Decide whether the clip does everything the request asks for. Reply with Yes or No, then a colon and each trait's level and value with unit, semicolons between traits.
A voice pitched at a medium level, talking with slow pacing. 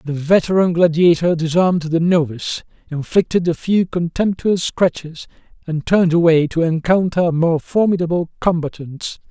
Yes: medium, 170 Hz; slow, 125 wpm